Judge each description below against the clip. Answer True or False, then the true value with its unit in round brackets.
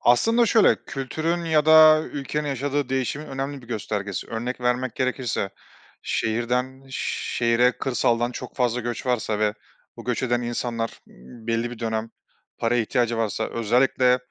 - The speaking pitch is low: True (125 Hz)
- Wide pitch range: False (2.7 semitones)